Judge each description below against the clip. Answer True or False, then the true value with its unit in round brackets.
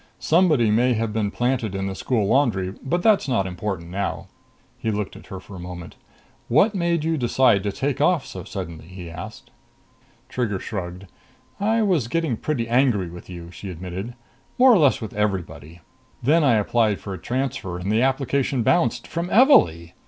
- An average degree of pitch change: False (6.8 semitones)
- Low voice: True (110 Hz)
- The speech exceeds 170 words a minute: True (180 wpm)